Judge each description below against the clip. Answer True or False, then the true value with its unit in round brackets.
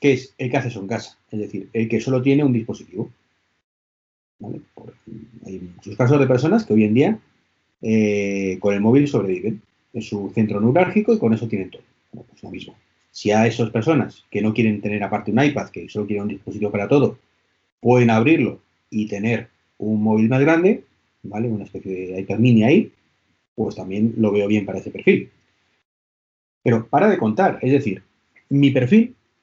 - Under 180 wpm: False (190 wpm)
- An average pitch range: True (3.8 semitones)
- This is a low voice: True (110 Hz)